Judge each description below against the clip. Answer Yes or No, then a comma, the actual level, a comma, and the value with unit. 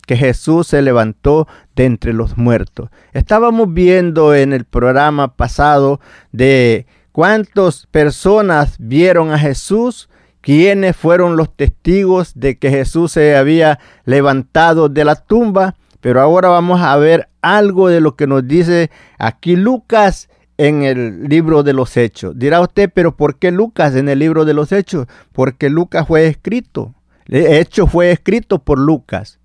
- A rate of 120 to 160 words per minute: Yes, average, 150 wpm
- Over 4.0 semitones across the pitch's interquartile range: Yes, average, 4.7 semitones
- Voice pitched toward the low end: No, medium, 150 Hz